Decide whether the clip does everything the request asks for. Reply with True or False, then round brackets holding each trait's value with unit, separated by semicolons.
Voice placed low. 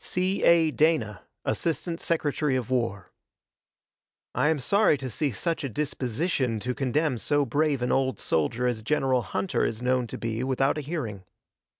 True (130 Hz)